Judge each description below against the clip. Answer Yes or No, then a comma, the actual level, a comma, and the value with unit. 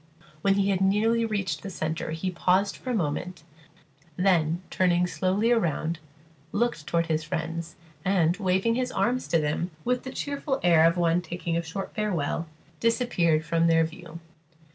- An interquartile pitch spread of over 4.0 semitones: No, average, 3.6 semitones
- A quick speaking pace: No, average, 165 wpm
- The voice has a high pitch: No, medium, 180 Hz